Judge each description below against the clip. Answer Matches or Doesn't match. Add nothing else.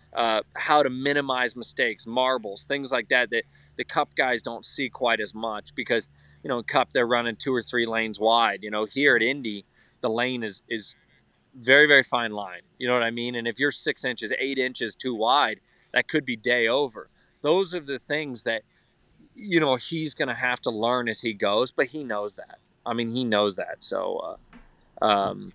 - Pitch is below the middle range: Matches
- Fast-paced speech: Matches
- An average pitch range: Matches